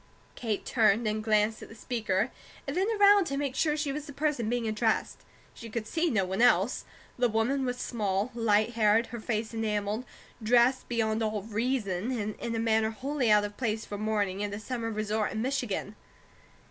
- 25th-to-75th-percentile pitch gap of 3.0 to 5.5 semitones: No, narrow, 2.6 semitones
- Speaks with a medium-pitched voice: No, high, 225 Hz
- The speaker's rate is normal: Yes, average, 195 wpm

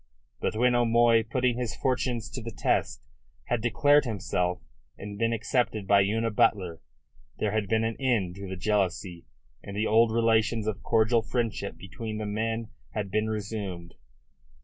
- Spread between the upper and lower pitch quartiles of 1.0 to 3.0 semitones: Yes, narrow, 2.5 semitones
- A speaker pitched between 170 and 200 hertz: No, low, 110 Hz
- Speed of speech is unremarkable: Yes, average, 160 wpm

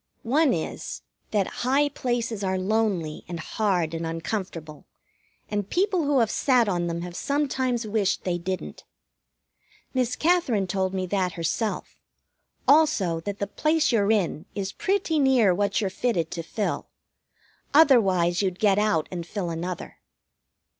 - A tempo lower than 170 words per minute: Yes, average, 145 wpm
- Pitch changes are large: Yes, wide, 6.0 semitones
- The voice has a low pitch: No, high, 200 Hz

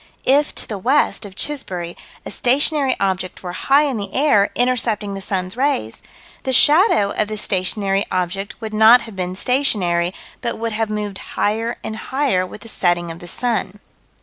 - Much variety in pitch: No, average, 5.0 semitones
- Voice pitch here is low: No, high, 210 Hz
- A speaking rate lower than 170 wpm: No, average, 175 wpm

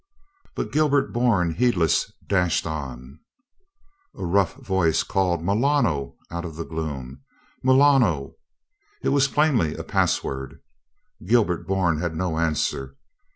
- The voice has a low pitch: Yes, very low, 85 Hz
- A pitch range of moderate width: No, wide, 7.0 semitones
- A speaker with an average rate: No, slow, 115 wpm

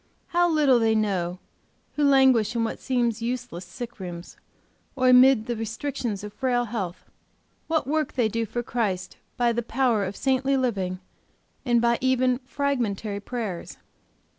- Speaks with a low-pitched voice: No, high, 235 Hz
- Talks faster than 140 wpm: Yes, average, 150 wpm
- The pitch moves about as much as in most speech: Yes, average, 3.7 semitones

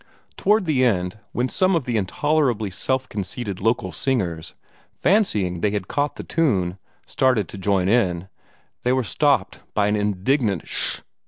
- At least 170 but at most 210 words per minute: No, average, 160 wpm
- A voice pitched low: Yes, low, 110 Hz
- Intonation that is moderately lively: No, wide, 5.7 semitones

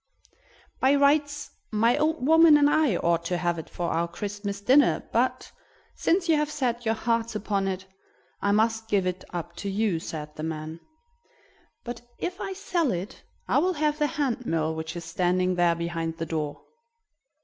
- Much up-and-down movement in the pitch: Yes, wide, 9.0 semitones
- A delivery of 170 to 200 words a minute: Yes, average, 180 wpm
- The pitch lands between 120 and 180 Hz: No, high, 205 Hz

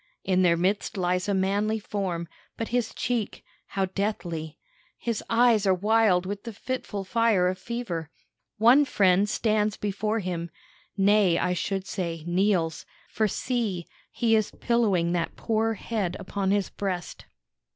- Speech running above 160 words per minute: No, average, 145 wpm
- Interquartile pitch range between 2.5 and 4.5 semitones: Yes, average, 3.4 semitones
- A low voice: No, high, 200 Hz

